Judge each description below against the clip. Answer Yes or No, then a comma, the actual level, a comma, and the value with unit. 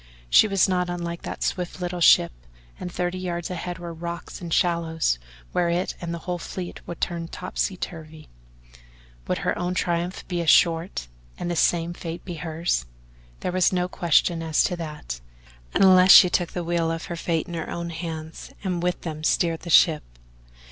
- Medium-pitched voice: Yes, medium, 170 Hz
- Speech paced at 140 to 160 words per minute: No, average, 185 wpm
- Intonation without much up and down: Yes, narrow, 1.5 semitones